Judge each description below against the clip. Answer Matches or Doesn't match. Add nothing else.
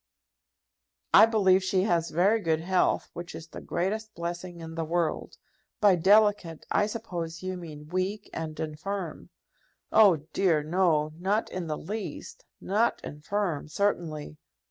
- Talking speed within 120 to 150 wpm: Matches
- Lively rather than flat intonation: Doesn't match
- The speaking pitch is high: Doesn't match